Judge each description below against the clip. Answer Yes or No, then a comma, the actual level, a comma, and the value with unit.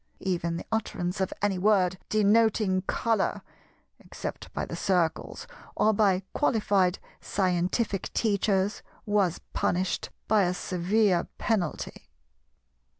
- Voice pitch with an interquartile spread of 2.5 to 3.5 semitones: Yes, average, 2.8 semitones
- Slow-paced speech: Yes, slow, 105 wpm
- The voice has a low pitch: No, high, 195 Hz